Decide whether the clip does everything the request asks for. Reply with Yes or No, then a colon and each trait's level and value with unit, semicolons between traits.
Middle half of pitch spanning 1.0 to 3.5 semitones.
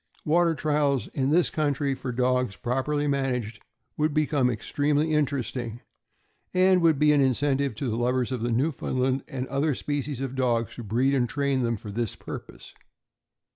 Yes: average, 3.0 semitones